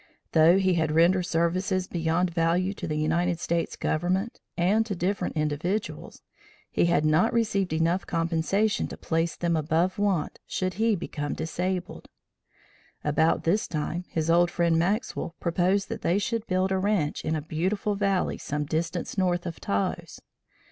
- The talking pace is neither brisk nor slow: Yes, average, 155 wpm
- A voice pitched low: No, medium, 175 Hz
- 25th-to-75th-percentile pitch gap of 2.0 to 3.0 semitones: Yes, average, 2.7 semitones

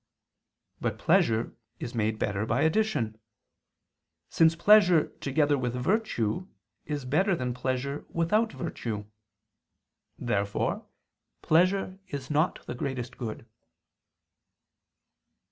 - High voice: No, medium, 140 Hz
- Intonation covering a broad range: Yes, wide, 6.4 semitones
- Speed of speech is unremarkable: No, slow, 95 wpm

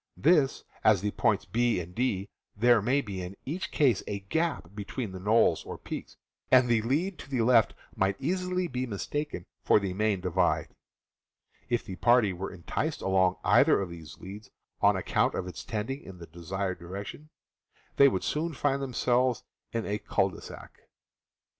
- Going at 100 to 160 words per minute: No, average, 175 wpm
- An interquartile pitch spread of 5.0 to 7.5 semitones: Yes, wide, 5.5 semitones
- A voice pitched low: Yes, low, 110 Hz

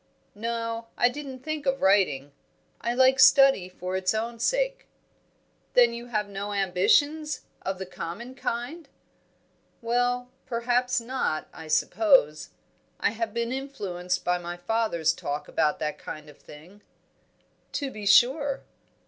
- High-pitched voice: Yes, high, 230 Hz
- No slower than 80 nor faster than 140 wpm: Yes, slow, 135 wpm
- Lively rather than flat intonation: Yes, wide, 6.0 semitones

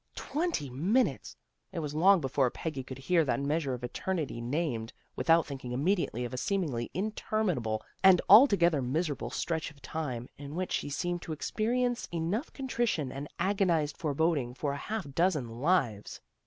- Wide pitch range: Yes, wide, 5.8 semitones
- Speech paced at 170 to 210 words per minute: No, average, 155 wpm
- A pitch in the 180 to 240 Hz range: No, medium, 155 Hz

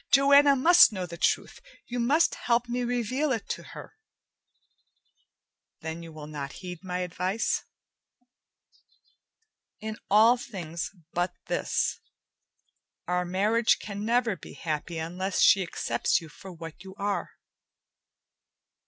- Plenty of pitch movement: Yes, wide, 5.7 semitones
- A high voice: Yes, high, 195 Hz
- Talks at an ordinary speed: No, slow, 125 wpm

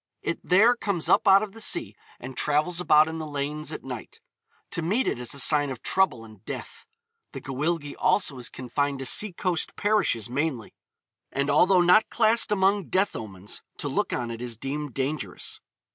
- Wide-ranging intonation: Yes, wide, 6.5 semitones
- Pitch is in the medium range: Yes, medium, 150 Hz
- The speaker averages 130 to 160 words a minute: No, average, 190 wpm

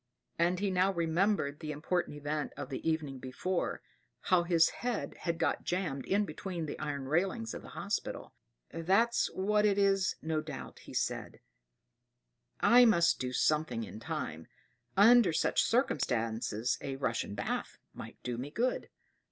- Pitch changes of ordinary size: No, wide, 5.8 semitones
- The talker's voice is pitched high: No, medium, 165 Hz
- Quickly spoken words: No, average, 150 wpm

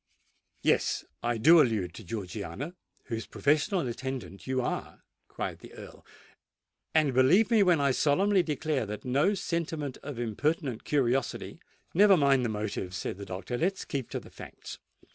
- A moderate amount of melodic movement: No, wide, 5.8 semitones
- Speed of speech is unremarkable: Yes, average, 155 wpm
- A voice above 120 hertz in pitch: Yes, low, 135 Hz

